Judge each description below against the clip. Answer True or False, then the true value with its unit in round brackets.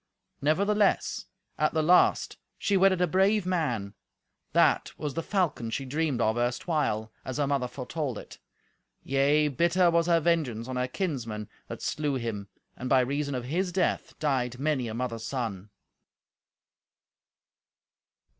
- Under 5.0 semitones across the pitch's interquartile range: False (5.5 semitones)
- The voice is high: False (140 Hz)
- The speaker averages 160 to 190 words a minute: False (145 wpm)